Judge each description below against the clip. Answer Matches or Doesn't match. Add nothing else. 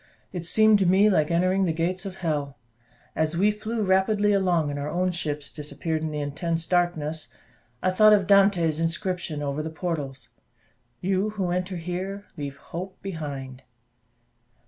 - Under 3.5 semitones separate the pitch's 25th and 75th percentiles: Doesn't match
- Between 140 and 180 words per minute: Matches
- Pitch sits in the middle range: Matches